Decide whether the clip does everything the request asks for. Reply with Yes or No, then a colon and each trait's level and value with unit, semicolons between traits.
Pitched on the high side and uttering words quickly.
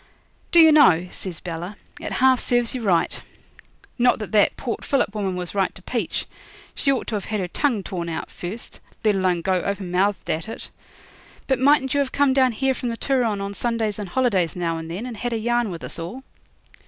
Yes: high, 210 Hz; fast, 215 wpm